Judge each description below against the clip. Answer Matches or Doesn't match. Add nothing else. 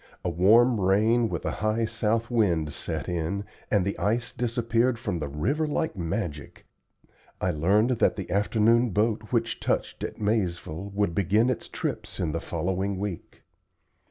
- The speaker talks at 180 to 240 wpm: Doesn't match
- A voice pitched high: Doesn't match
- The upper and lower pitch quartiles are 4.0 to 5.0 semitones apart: Matches